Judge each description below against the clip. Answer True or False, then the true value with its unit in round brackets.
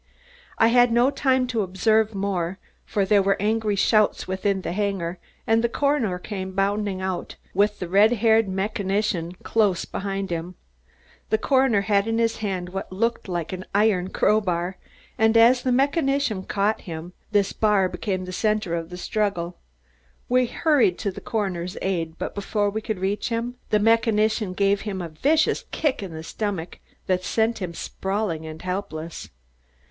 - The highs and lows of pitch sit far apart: False (3.2 semitones)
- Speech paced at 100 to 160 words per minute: False (170 wpm)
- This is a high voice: True (200 Hz)